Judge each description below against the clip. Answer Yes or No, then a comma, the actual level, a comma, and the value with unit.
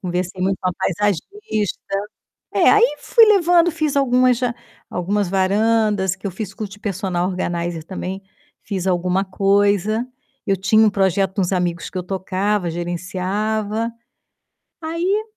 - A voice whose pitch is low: No, high, 195 Hz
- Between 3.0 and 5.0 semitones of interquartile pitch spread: Yes, average, 3.3 semitones